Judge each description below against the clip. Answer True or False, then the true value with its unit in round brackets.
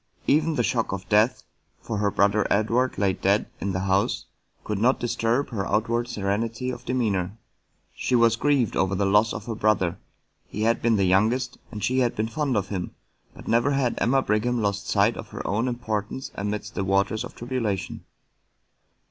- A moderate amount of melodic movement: True (3.2 semitones)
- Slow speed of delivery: False (185 wpm)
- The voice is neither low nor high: False (110 Hz)